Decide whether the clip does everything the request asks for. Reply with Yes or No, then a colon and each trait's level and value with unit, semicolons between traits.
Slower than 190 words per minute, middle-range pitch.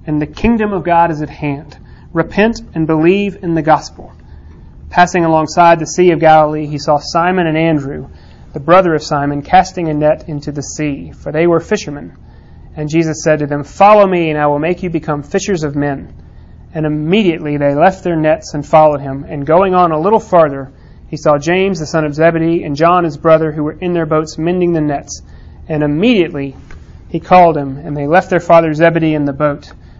No: fast, 205 wpm; medium, 155 Hz